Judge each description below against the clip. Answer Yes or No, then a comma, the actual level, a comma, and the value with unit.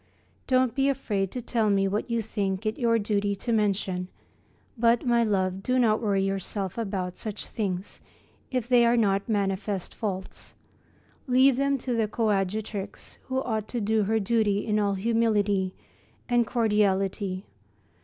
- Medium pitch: No, high, 215 Hz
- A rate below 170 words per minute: Yes, average, 155 wpm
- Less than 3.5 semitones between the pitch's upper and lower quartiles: Yes, average, 3.0 semitones